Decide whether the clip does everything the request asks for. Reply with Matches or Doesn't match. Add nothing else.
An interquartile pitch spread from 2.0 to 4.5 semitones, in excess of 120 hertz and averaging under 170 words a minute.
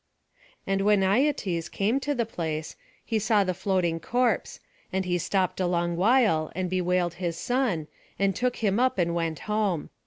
Doesn't match